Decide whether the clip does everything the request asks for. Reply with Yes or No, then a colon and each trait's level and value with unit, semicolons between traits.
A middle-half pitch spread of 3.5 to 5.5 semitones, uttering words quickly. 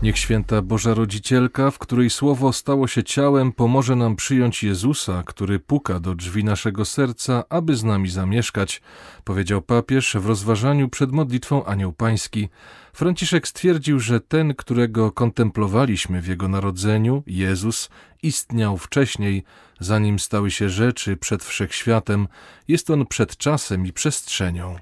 No: average, 5.2 semitones; average, 135 wpm